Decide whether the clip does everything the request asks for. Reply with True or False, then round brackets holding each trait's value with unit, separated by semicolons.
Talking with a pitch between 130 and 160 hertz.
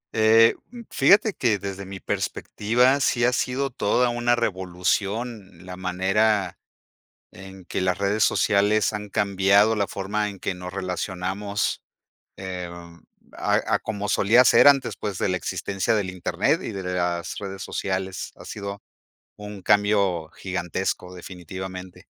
False (100 Hz)